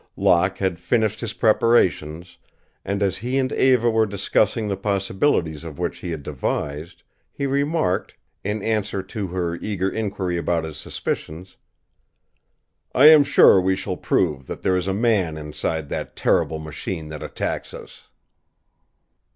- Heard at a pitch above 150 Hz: No, very low, 95 Hz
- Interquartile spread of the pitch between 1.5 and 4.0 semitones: No, average, 4.7 semitones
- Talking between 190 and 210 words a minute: No, average, 150 wpm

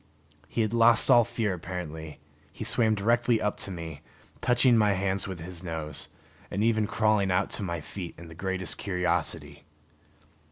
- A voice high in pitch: No, very low, 95 Hz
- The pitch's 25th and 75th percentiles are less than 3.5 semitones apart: No, average, 4.3 semitones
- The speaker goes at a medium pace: Yes, average, 165 wpm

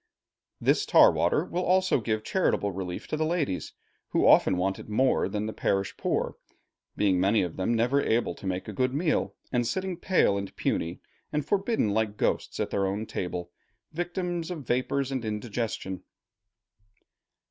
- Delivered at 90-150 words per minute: No, average, 170 wpm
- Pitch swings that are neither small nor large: No, wide, 7.9 semitones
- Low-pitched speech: Yes, low, 115 Hz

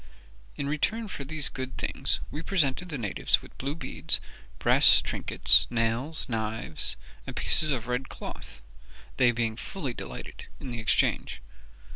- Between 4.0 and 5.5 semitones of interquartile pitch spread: Yes, average, 4.7 semitones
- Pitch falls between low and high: No, low, 130 Hz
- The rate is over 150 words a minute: No, average, 145 wpm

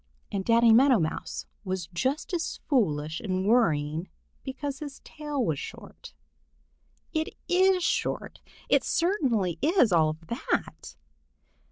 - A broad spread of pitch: Yes, wide, 9.0 semitones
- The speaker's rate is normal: No, slow, 125 wpm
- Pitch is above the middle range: Yes, high, 230 Hz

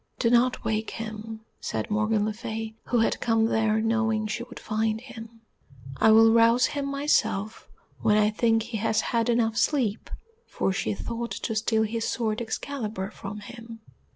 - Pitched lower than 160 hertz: No, high, 225 Hz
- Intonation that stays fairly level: Yes, narrow, 1.4 semitones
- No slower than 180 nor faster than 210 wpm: No, average, 170 wpm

